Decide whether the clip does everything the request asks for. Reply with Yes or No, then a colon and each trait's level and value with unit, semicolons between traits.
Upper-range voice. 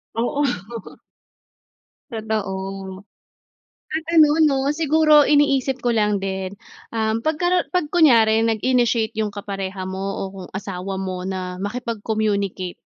Yes: high, 220 Hz